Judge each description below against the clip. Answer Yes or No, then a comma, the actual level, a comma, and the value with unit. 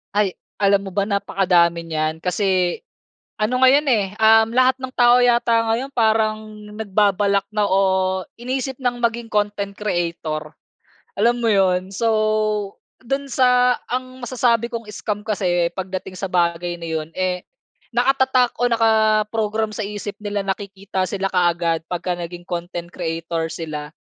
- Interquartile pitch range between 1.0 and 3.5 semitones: No, average, 4.2 semitones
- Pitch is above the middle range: Yes, high, 205 Hz